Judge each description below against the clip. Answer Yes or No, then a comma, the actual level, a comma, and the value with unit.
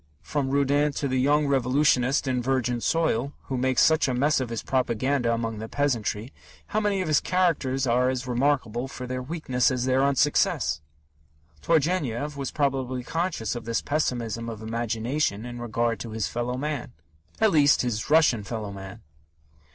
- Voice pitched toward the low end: Yes, low, 130 Hz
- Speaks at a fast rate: No, average, 165 wpm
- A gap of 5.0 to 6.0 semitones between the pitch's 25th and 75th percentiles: No, average, 3.4 semitones